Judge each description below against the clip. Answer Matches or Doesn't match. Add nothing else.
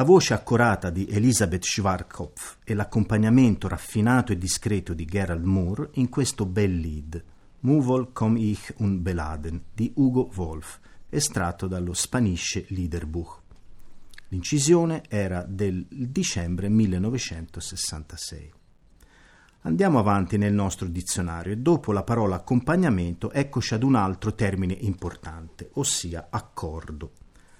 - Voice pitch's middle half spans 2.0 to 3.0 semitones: Doesn't match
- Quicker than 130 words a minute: Doesn't match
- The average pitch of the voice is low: Matches